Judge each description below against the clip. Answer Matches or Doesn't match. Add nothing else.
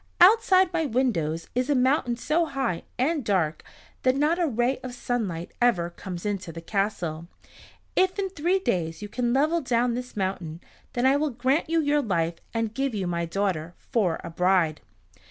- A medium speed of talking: Matches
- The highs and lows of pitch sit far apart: Matches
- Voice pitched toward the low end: Doesn't match